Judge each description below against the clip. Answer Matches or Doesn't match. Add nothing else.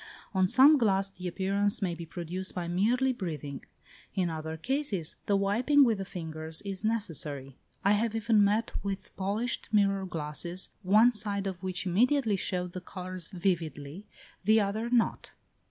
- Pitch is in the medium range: Doesn't match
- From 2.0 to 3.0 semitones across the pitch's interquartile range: Doesn't match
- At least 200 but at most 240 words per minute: Doesn't match